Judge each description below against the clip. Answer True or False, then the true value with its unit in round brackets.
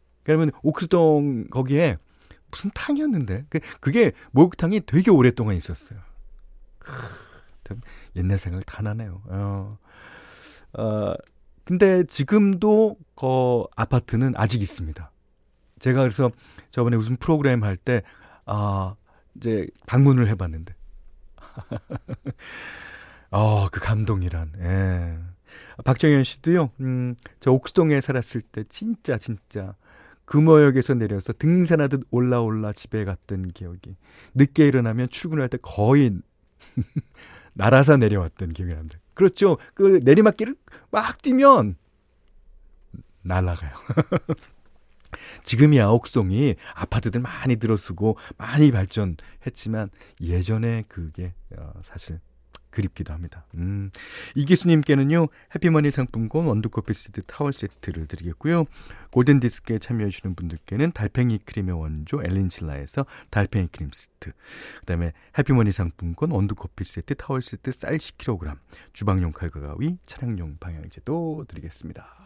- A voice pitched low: True (110 Hz)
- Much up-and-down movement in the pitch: True (7.1 semitones)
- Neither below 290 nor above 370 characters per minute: False (275 characters per minute)